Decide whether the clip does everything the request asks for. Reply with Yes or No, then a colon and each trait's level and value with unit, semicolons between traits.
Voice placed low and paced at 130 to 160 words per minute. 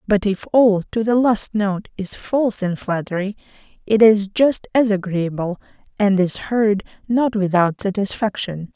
No: high, 205 Hz; average, 150 wpm